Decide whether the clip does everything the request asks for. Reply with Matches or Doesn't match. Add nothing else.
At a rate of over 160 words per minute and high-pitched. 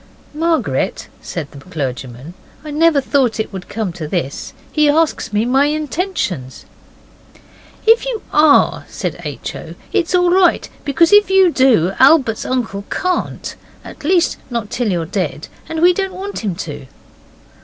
Doesn't match